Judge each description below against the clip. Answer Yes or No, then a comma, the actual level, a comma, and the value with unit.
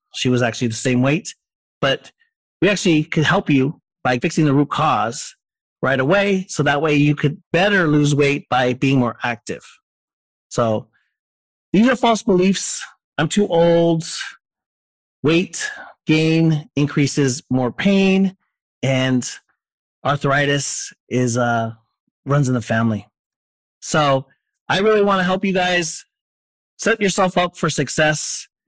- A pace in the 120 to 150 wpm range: Yes, slow, 135 wpm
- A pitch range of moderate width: No, wide, 6.0 semitones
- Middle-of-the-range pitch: Yes, medium, 150 Hz